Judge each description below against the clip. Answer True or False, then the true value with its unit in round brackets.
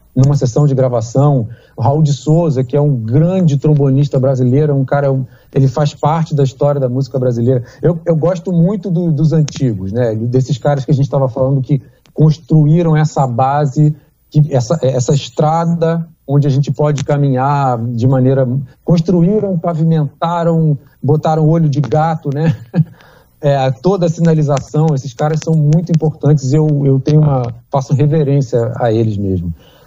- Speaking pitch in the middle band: True (145 Hz)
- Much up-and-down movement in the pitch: False (3.0 semitones)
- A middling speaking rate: True (160 wpm)